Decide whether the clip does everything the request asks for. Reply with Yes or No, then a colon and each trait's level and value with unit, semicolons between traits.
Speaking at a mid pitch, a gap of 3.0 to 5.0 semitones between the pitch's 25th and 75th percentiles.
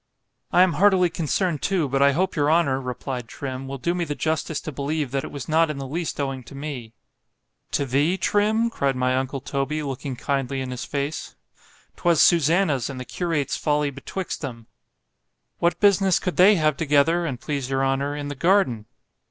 Yes: medium, 145 Hz; average, 4.1 semitones